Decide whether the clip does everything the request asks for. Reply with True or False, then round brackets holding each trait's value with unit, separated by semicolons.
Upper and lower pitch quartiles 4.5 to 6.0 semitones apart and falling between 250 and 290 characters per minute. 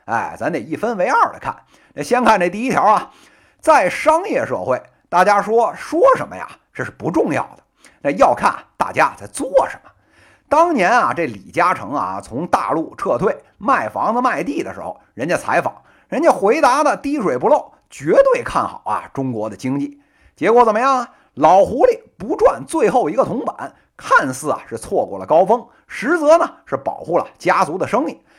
False (7.6 semitones; 265 characters per minute)